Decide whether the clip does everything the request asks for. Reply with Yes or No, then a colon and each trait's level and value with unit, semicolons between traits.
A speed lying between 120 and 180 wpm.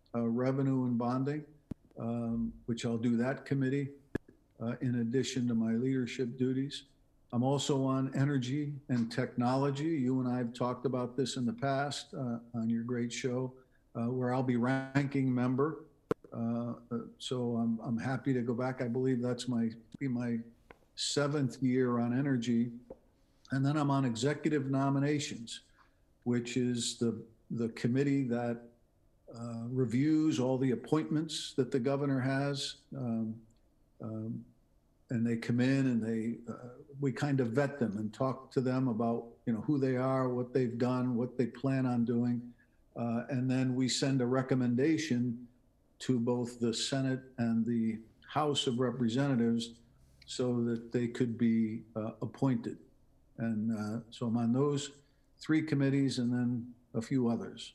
Yes: average, 155 wpm